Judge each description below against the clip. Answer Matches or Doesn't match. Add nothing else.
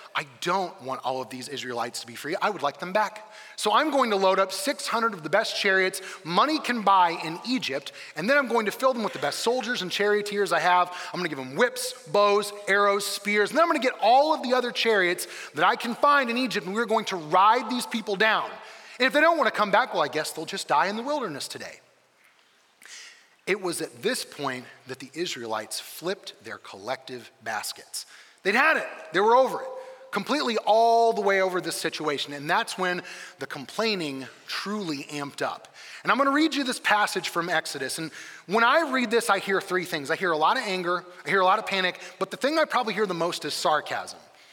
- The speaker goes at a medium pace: Doesn't match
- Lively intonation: Matches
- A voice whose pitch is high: Matches